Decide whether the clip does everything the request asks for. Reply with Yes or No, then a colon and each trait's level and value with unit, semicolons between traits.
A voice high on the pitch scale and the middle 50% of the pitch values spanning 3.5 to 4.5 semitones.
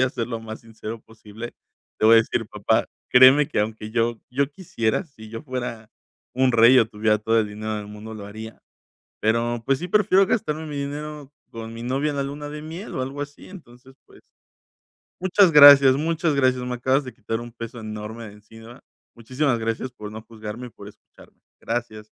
No: low, 120 Hz; average, 4.1 semitones